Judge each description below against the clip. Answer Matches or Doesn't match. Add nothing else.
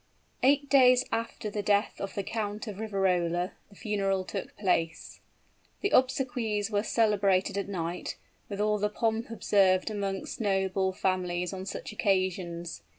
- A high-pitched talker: Matches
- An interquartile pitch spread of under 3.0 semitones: Matches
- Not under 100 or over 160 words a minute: Matches